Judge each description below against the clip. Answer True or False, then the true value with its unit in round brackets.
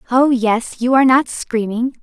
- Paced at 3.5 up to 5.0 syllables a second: True (4.6 syllables/s)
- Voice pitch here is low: False (245 Hz)